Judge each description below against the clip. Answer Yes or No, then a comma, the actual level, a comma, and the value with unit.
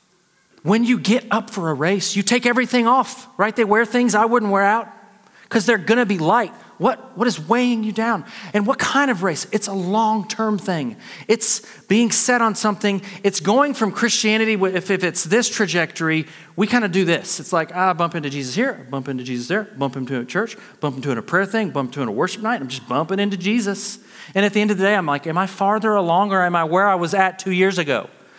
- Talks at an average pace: No, fast, 240 wpm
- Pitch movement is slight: No, average, 3.9 semitones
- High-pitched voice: Yes, high, 205 Hz